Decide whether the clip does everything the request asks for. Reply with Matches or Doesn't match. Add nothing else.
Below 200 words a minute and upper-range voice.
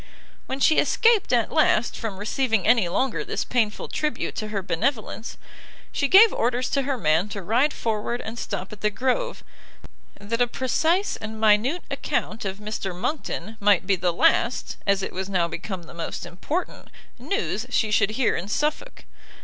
Matches